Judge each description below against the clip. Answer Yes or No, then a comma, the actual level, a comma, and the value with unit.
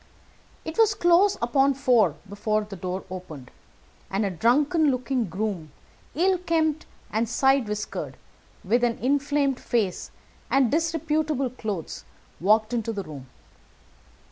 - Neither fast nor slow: No, slow, 125 wpm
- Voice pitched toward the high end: Yes, high, 240 Hz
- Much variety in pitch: Yes, wide, 6.2 semitones